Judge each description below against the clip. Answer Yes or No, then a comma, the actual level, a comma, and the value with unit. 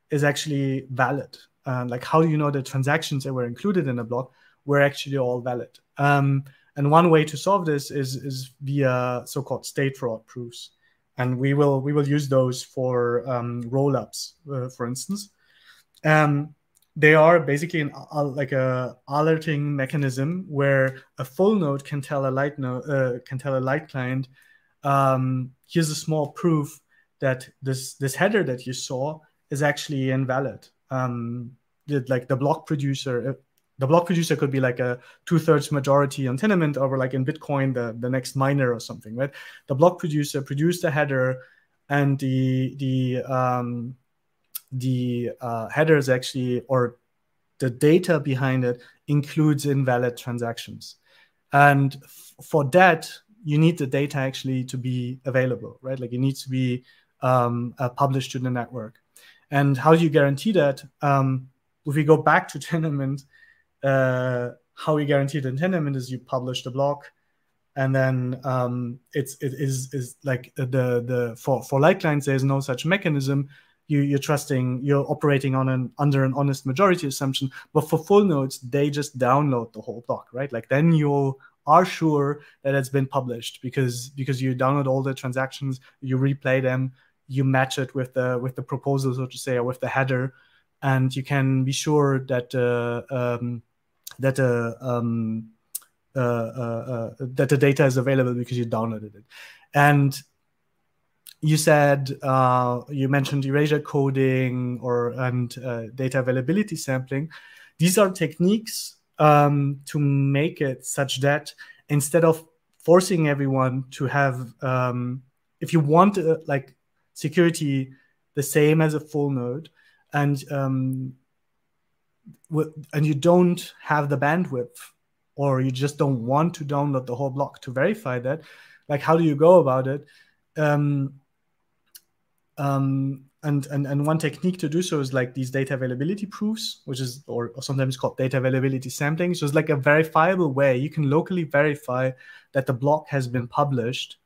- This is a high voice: No, low, 135 Hz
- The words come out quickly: No, average, 165 wpm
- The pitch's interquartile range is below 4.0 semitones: Yes, narrow, 2.5 semitones